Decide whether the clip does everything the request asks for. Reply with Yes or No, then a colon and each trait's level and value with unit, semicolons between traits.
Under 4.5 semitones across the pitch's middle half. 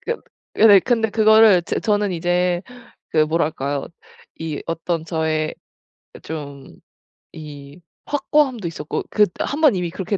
No: wide, 5.5 semitones